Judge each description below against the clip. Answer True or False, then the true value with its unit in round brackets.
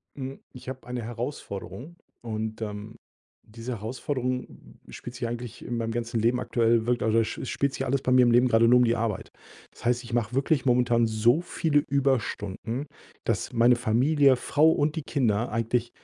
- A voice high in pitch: False (120 Hz)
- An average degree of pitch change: False (2.2 semitones)